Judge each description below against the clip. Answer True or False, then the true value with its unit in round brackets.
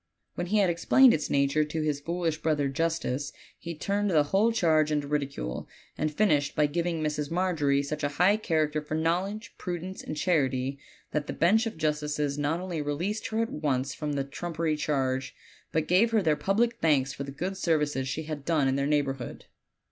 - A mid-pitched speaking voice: True (155 Hz)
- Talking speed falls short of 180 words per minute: False (195 wpm)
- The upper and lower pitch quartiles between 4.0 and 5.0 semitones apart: False (3.4 semitones)